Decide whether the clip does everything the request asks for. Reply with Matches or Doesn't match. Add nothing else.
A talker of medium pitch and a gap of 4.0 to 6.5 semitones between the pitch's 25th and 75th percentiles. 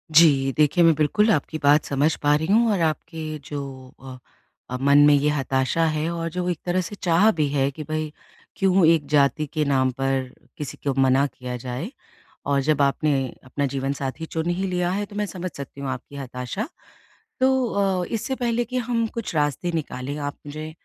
Matches